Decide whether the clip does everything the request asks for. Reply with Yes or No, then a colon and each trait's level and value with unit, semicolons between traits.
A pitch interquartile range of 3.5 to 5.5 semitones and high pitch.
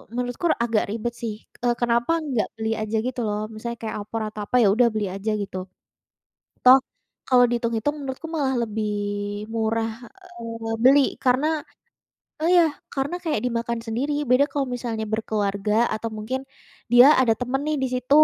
No: average, 2.9 semitones; high, 235 Hz